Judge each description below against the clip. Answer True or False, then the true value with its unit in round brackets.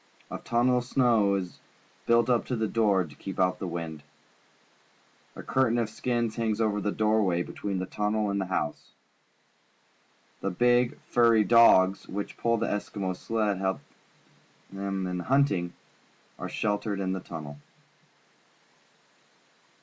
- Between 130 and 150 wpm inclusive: True (145 wpm)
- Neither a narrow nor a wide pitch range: True (3.7 semitones)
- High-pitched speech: False (105 Hz)